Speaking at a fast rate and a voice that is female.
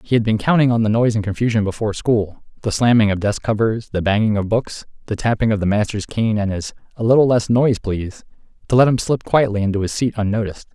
No: fast, 225 wpm; male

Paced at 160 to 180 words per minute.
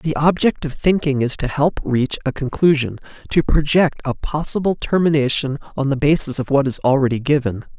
Yes: average, 175 wpm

